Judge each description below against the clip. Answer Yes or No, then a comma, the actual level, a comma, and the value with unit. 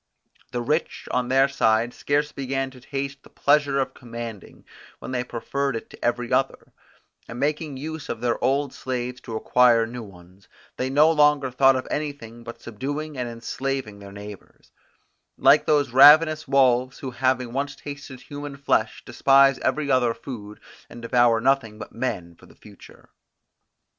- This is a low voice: Yes, low, 130 Hz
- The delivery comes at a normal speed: Yes, average, 165 wpm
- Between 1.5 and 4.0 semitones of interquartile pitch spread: Yes, average, 3.0 semitones